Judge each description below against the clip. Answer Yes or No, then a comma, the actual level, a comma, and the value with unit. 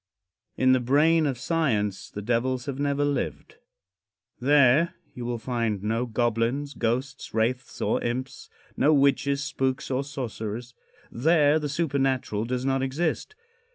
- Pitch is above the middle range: No, low, 130 Hz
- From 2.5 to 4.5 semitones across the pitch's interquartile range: Yes, average, 3.1 semitones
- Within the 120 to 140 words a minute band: Yes, slow, 135 wpm